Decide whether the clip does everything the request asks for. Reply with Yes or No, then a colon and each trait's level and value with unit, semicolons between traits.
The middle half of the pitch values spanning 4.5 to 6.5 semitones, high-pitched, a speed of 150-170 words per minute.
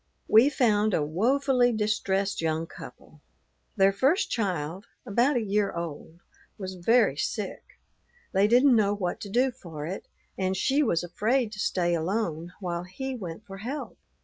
Yes: average, 5.2 semitones; high, 200 Hz; average, 155 wpm